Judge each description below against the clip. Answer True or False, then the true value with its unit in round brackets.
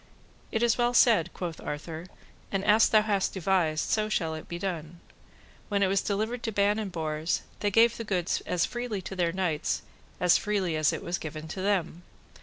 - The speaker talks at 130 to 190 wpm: False (200 wpm)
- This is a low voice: False (190 Hz)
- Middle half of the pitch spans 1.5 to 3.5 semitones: False (4.0 semitones)